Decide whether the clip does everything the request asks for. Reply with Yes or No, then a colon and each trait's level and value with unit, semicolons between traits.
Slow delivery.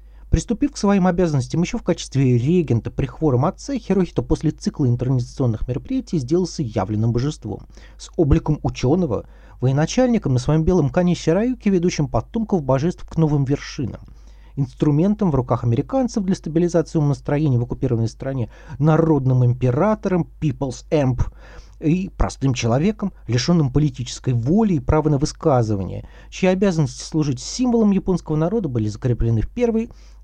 No: average, 135 wpm